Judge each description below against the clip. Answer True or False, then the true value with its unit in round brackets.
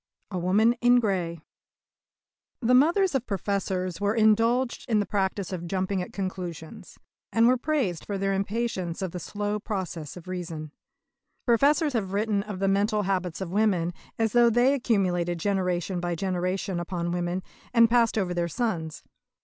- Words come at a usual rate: True (160 wpm)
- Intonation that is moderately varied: True (4.1 semitones)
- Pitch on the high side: True (195 Hz)